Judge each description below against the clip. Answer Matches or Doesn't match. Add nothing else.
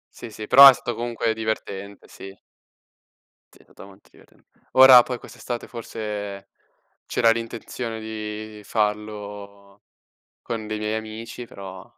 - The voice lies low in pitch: Matches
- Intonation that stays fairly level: Matches